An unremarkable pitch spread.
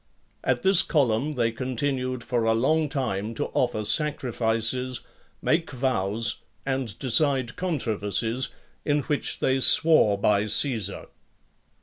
Yes: average, 4.0 semitones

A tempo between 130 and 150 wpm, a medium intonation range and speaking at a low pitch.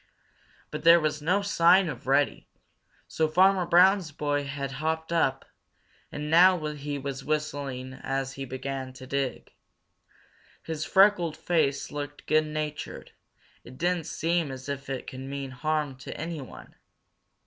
No: average, 140 wpm; average, 3.3 semitones; medium, 150 Hz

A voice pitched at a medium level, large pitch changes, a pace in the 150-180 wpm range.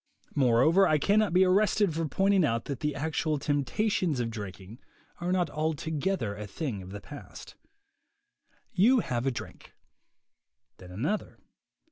No: medium, 150 Hz; wide, 7.7 semitones; average, 140 wpm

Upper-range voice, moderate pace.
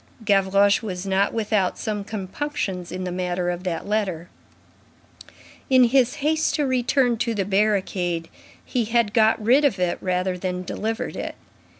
Yes: high, 200 Hz; average, 155 wpm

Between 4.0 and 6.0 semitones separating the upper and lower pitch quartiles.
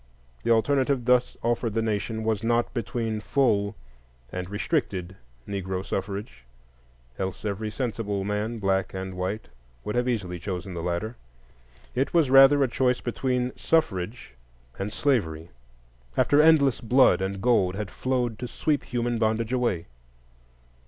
Yes: average, 4.3 semitones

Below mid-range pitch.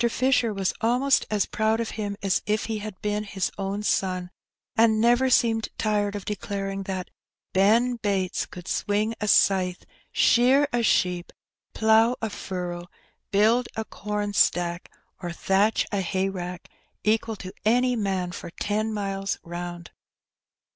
No: high, 205 Hz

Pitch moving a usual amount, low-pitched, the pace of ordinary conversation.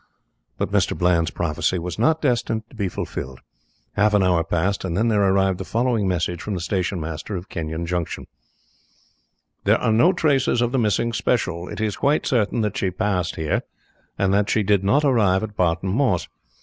Yes: average, 4.2 semitones; low, 100 Hz; average, 190 wpm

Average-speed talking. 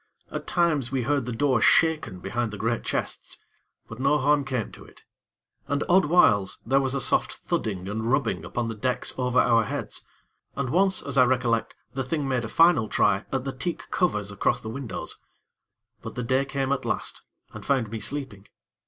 Yes: average, 195 wpm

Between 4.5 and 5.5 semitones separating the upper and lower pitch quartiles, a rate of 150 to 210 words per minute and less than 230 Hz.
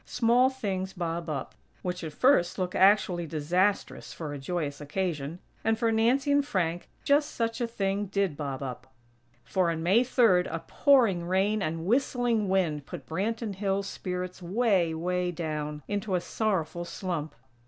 Yes: average, 4.8 semitones; average, 160 wpm; medium, 185 Hz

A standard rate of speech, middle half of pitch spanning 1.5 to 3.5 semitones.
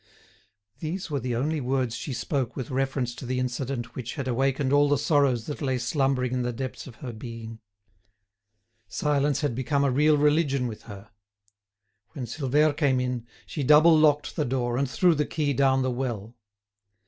Yes: average, 180 wpm; average, 2.9 semitones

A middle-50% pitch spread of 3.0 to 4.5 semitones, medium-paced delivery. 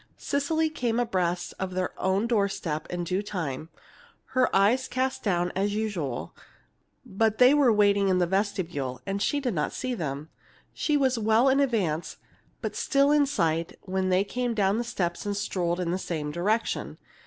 No: wide, 5.6 semitones; average, 175 wpm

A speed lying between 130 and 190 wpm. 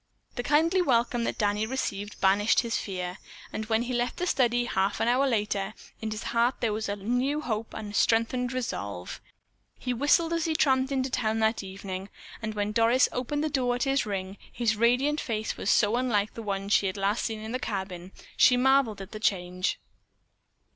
No: average, 200 wpm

